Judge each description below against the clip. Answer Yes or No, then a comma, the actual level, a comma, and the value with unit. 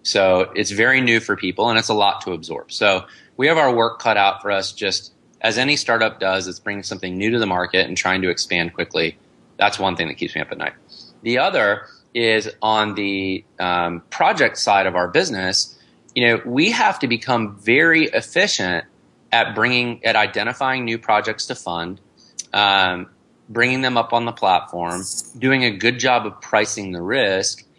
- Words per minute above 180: Yes, average, 190 wpm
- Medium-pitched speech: No, low, 105 Hz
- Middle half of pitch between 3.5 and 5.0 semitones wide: Yes, average, 4.2 semitones